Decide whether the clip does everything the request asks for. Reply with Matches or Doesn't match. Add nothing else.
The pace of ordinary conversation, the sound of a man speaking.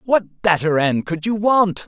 Matches